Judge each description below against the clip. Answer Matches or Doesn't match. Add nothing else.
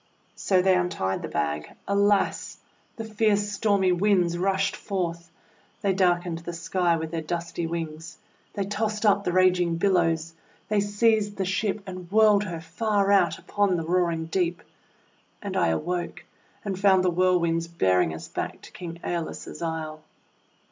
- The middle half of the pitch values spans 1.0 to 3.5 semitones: Matches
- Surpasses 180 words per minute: Doesn't match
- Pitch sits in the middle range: Matches